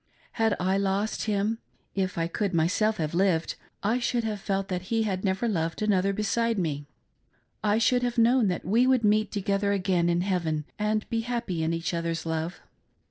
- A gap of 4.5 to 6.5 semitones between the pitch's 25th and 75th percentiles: No, average, 4.0 semitones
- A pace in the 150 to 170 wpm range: No, average, 195 wpm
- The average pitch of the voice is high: Yes, high, 200 Hz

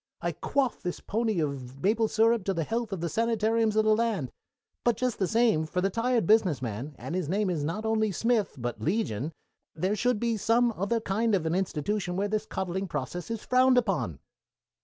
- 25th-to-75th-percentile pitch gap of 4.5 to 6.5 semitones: Yes, average, 5.3 semitones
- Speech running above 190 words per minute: Yes, average, 200 wpm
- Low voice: No, high, 205 Hz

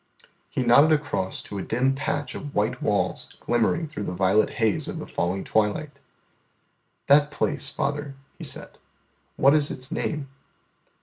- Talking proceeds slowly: No, average, 150 wpm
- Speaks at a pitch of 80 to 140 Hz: Yes, low, 135 Hz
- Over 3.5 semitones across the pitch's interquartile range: Yes, wide, 5.5 semitones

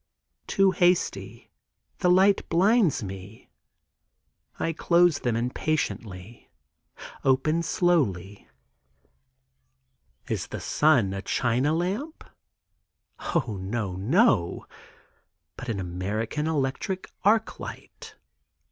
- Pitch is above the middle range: No, medium, 140 Hz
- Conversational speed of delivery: No, slow, 85 wpm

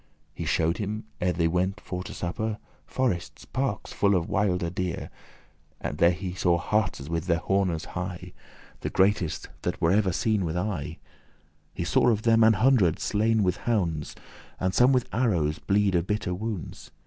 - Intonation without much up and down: No, average, 3.8 semitones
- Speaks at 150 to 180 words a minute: Yes, average, 165 wpm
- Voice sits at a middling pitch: No, very low, 95 Hz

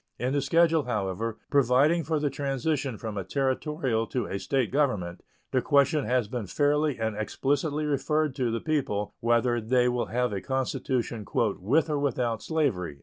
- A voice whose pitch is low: Yes, low, 130 Hz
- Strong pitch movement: No, average, 4.3 semitones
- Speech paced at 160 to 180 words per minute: Yes, average, 165 wpm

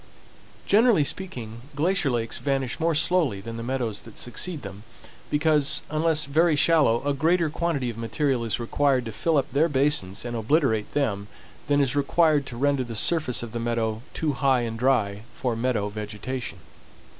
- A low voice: Yes, low, 130 Hz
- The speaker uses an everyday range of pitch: Yes, average, 4.7 semitones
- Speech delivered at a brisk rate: No, average, 170 wpm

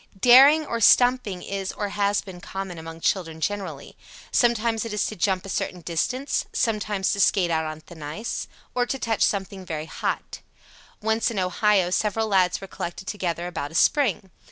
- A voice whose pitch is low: No, high, 195 Hz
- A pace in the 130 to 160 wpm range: No, average, 180 wpm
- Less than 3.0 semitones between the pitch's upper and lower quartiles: No, average, 3.9 semitones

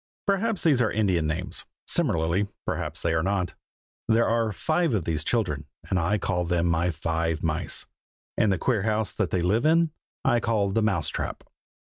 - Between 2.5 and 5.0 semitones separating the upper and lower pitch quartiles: No, wide, 5.5 semitones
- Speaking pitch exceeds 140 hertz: No, low, 100 Hz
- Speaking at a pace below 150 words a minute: No, average, 180 wpm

